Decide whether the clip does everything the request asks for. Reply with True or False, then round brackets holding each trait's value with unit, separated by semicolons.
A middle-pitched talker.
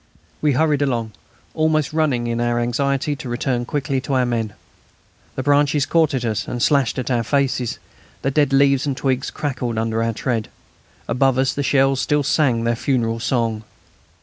False (130 Hz)